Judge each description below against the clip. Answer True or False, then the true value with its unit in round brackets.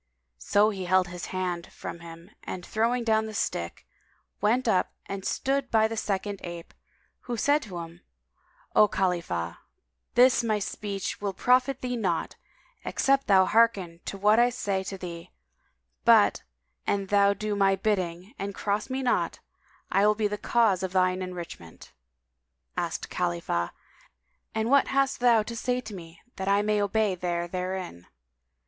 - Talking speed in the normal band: True (165 wpm)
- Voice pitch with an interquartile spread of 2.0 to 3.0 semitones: False (3.6 semitones)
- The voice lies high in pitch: True (200 Hz)